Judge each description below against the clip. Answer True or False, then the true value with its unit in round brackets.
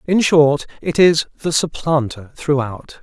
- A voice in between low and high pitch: True (150 Hz)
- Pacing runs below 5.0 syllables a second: True (4.0 syllables/s)